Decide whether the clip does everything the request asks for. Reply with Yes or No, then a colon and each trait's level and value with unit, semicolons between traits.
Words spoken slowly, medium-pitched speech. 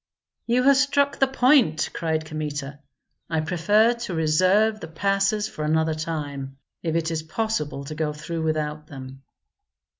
No: average, 150 wpm; medium, 160 Hz